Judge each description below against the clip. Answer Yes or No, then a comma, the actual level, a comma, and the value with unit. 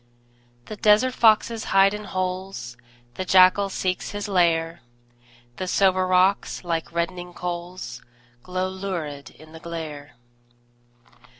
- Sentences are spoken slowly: Yes, slow, 115 wpm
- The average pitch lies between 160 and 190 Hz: Yes, medium, 185 Hz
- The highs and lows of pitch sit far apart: No, narrow, 2.4 semitones